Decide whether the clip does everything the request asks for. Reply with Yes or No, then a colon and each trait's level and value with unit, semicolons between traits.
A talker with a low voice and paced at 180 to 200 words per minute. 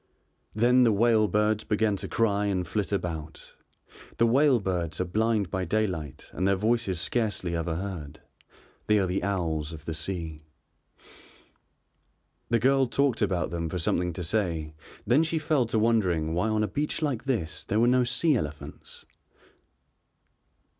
No: low, 100 Hz; average, 160 wpm